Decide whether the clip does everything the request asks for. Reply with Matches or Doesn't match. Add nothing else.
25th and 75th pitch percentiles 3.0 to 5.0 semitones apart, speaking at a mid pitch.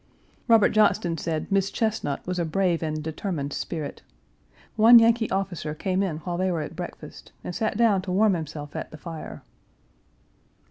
Matches